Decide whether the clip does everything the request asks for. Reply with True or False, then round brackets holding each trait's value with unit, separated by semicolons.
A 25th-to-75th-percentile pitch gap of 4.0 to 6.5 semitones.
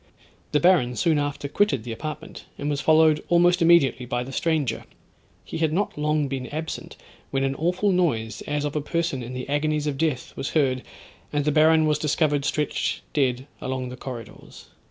False (3.2 semitones)